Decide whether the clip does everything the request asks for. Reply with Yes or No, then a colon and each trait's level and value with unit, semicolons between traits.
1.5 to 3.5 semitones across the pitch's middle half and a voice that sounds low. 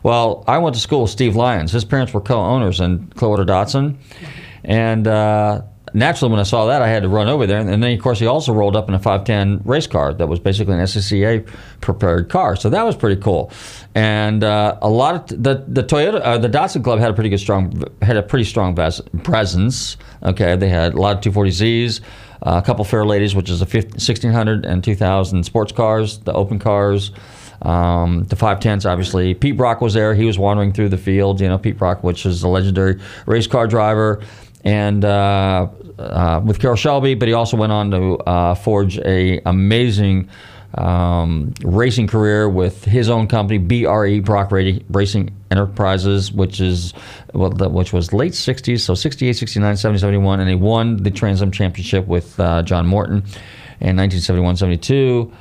Yes: average, 3.1 semitones; low, 105 Hz